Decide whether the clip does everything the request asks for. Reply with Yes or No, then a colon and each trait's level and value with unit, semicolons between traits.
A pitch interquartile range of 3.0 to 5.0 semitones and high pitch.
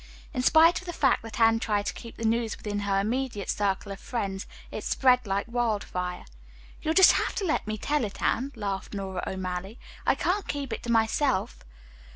Yes: average, 4.5 semitones; high, 225 Hz